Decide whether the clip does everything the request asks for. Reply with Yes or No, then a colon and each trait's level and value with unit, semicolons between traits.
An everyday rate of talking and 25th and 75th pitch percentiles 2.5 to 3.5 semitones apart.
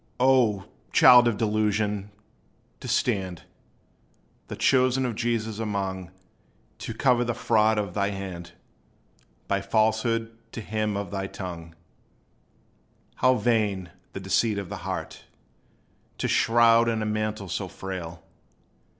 No: slow, 125 wpm; average, 2.9 semitones